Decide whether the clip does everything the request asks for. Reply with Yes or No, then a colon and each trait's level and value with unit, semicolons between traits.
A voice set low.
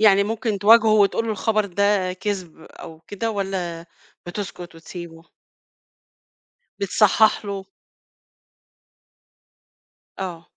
No: high, 200 Hz